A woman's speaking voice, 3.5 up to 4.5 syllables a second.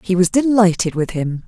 No: female; 5.1 syllables/s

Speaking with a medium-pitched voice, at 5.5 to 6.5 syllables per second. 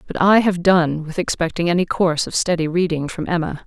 Yes: medium, 170 Hz; 5.7 syllables/s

